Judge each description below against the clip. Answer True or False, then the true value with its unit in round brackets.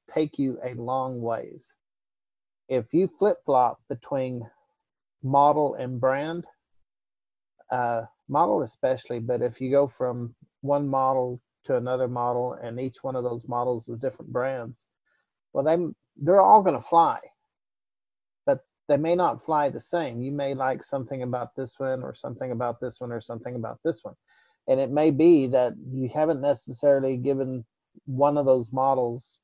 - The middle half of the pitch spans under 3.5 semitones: True (2.5 semitones)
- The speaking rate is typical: True (160 wpm)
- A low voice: True (130 Hz)